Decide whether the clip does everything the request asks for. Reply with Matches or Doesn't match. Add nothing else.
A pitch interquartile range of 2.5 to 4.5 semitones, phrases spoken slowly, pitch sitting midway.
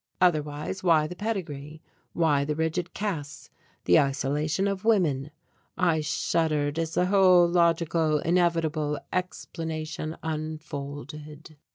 Matches